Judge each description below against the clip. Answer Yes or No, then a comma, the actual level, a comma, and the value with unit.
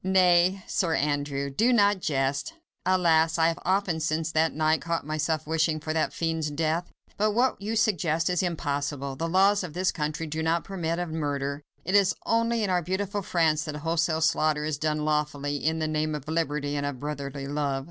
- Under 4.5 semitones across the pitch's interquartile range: Yes, average, 3.2 semitones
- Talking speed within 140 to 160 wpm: No, average, 195 wpm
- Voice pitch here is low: No, medium, 160 Hz